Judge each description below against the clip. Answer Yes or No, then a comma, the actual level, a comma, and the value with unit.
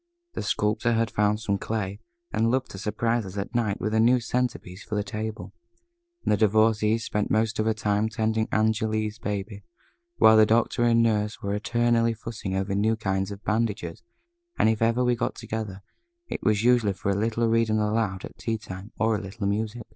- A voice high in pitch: No, low, 110 Hz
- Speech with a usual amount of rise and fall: No, narrow, 1.7 semitones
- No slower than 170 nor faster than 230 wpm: Yes, average, 200 wpm